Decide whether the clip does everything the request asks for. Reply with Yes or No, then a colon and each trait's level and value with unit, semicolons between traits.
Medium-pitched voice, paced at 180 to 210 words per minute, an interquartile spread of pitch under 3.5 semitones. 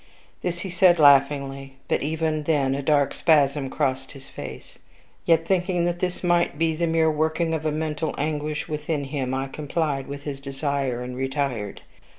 No: medium, 150 Hz; average, 165 wpm; average, 2.9 semitones